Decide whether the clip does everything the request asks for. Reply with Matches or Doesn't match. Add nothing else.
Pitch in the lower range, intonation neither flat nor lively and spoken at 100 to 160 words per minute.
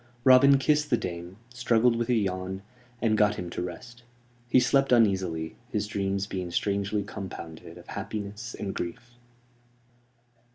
Matches